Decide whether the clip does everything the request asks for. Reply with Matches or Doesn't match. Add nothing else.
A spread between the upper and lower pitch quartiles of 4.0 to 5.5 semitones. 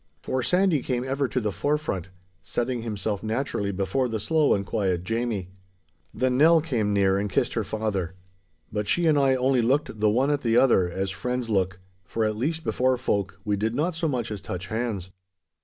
Matches